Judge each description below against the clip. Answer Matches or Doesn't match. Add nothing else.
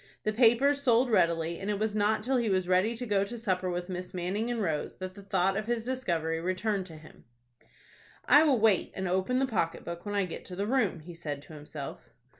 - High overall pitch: Matches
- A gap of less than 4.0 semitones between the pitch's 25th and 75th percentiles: Doesn't match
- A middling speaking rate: Doesn't match